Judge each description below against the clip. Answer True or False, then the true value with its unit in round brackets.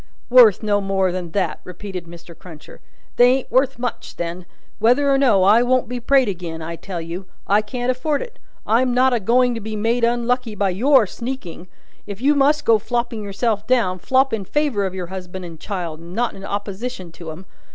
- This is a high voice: True (215 Hz)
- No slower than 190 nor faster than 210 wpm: True (205 wpm)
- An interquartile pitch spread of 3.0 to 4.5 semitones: False (5.2 semitones)